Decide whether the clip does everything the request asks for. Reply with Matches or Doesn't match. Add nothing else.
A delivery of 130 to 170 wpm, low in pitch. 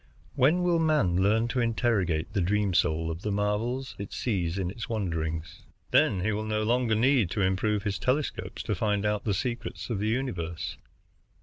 Doesn't match